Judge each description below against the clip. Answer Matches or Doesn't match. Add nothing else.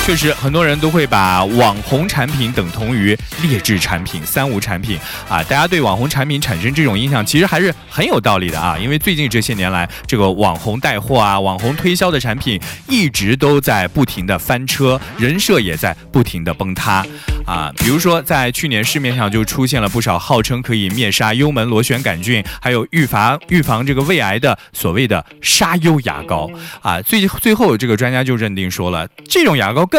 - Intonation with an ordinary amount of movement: Doesn't match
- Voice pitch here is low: Matches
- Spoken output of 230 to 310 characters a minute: Matches